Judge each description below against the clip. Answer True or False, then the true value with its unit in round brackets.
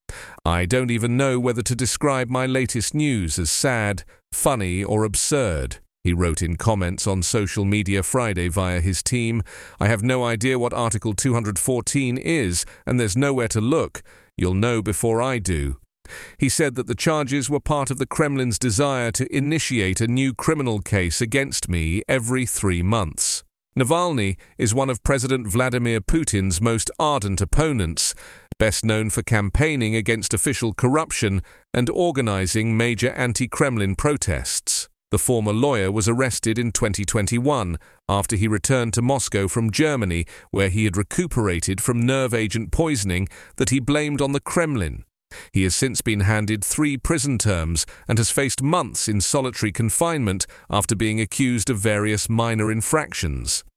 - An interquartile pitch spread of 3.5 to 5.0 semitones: True (4.7 semitones)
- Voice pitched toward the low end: True (115 Hz)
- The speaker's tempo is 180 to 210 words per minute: False (155 wpm)